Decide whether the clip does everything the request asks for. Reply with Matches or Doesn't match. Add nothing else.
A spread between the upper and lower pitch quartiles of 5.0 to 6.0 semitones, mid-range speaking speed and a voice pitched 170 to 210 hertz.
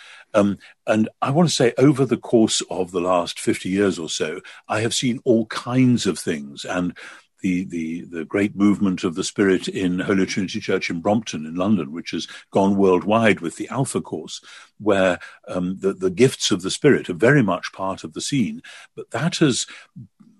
Doesn't match